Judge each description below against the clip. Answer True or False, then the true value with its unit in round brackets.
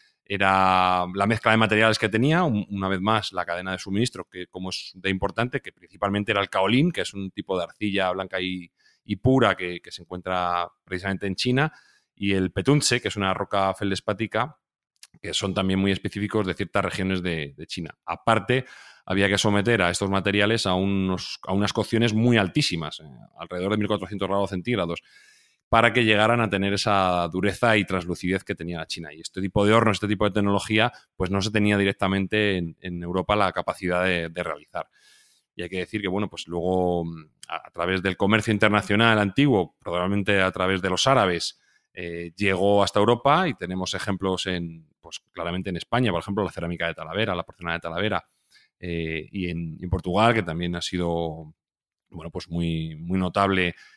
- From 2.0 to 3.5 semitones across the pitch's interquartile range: True (2.9 semitones)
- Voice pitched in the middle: False (95 Hz)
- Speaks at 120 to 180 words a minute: False (190 wpm)